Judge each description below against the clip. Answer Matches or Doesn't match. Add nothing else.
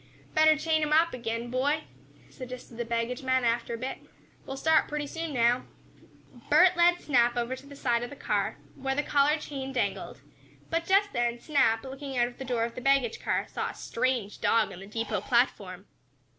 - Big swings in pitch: Doesn't match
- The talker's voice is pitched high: Matches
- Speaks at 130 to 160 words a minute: Doesn't match